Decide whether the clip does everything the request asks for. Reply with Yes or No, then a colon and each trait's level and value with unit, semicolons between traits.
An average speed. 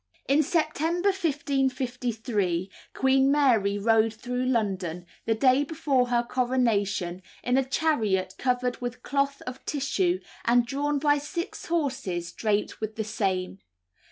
No: slow, 130 wpm